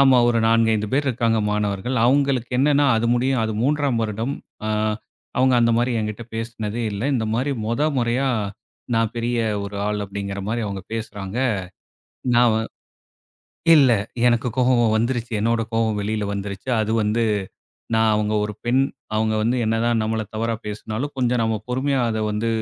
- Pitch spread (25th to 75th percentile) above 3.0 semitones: No, narrow, 2.4 semitones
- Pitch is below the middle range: Yes, low, 115 Hz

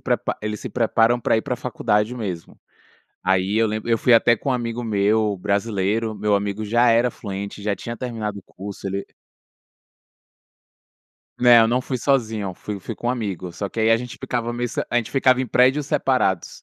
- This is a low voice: Yes, low, 115 Hz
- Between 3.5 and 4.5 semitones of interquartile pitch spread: No, average, 3.1 semitones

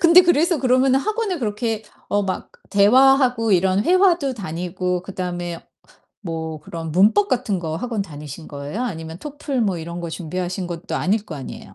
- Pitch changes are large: Yes, wide, 7.1 semitones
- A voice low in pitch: No, high, 195 Hz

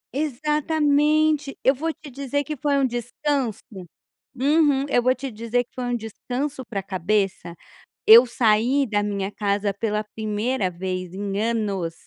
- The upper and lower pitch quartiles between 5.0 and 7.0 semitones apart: Yes, wide, 5.4 semitones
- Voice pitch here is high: Yes, high, 245 Hz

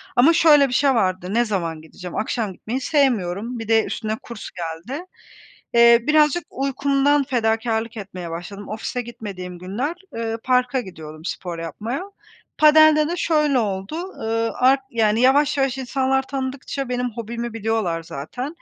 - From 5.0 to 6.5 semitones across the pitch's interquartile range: Yes, average, 5.3 semitones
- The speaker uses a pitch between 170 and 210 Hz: No, high, 235 Hz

